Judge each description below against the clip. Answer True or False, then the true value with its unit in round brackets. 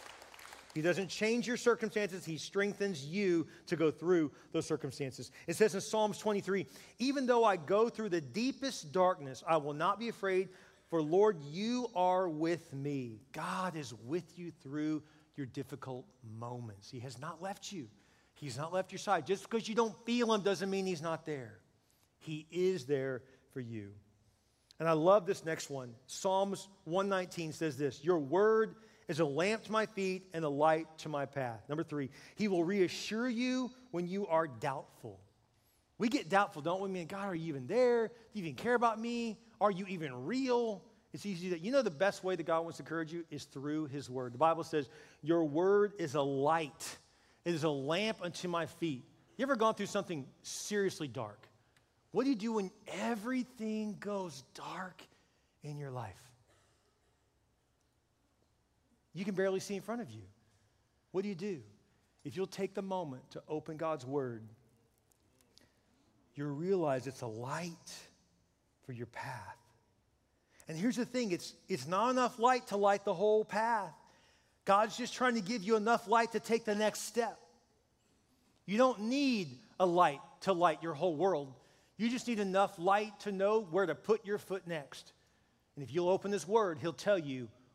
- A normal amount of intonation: False (6.3 semitones)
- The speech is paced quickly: False (185 wpm)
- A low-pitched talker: False (175 Hz)